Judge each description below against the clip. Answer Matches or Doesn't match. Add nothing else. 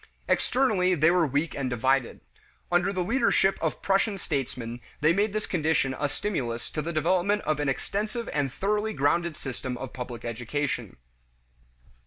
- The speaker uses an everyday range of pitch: Doesn't match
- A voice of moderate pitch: Matches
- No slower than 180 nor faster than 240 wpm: Doesn't match